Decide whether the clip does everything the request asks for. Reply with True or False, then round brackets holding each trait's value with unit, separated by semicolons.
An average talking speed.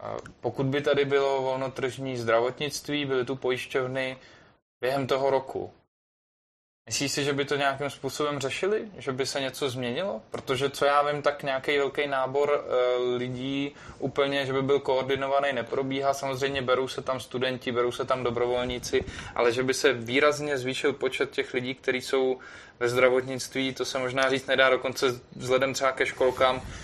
True (160 wpm)